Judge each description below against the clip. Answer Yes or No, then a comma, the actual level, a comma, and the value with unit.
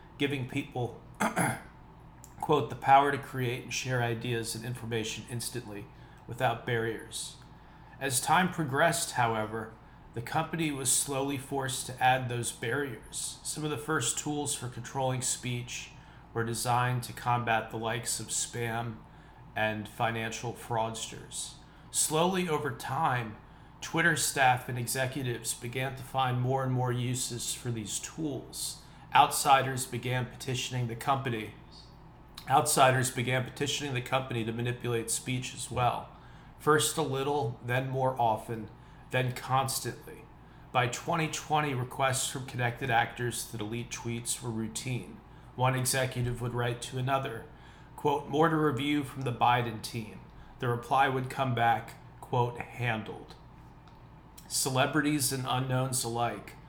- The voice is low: Yes, low, 125 Hz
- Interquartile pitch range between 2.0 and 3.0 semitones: Yes, narrow, 2.6 semitones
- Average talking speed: No, slow, 130 wpm